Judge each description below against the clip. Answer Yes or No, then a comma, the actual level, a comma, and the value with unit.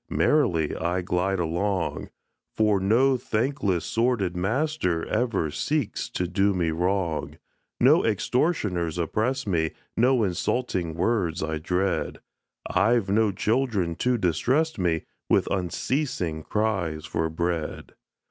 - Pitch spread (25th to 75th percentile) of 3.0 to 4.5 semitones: No, wide, 5.5 semitones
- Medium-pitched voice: No, very low, 95 Hz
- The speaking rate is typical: No, slow, 115 wpm